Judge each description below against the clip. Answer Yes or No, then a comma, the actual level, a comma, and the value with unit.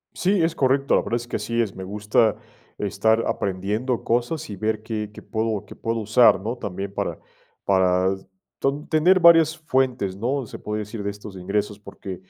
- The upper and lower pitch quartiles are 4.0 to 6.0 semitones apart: Yes, average, 4.4 semitones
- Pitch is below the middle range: Yes, low, 110 Hz